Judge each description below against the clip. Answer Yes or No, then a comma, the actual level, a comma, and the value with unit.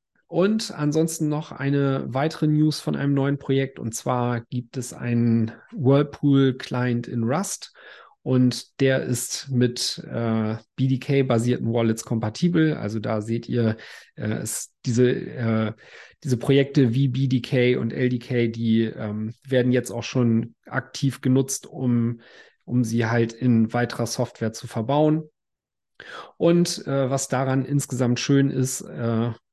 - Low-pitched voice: Yes, low, 125 Hz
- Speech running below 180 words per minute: Yes, average, 130 wpm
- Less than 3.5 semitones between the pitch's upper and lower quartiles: Yes, average, 2.8 semitones